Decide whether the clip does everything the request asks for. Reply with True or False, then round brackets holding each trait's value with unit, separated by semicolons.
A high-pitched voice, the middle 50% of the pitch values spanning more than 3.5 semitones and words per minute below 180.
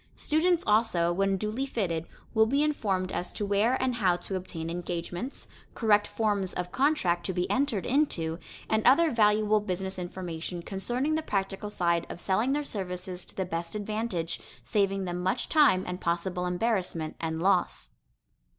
True (195 Hz; 4.2 semitones; 160 wpm)